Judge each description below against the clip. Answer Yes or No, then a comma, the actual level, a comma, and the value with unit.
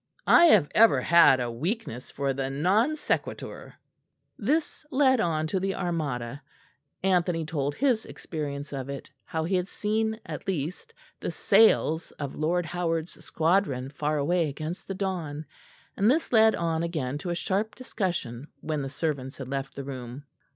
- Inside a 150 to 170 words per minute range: Yes, average, 160 wpm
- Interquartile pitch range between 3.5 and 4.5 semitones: No, wide, 5.4 semitones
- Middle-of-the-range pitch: Yes, medium, 165 Hz